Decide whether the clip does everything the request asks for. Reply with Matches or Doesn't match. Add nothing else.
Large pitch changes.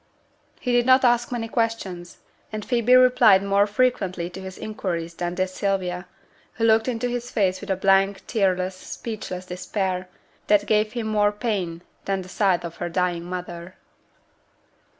Doesn't match